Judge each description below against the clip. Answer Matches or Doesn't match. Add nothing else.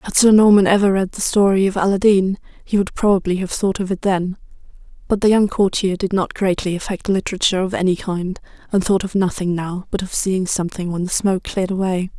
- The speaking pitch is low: Doesn't match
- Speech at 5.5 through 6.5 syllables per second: Matches